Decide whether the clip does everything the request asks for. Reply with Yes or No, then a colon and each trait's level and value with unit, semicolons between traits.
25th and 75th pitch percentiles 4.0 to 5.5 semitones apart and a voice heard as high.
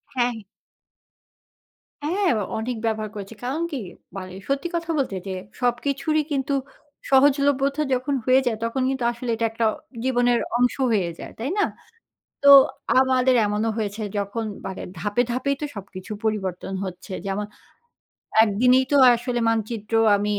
Yes: average, 4.3 semitones; high, 245 Hz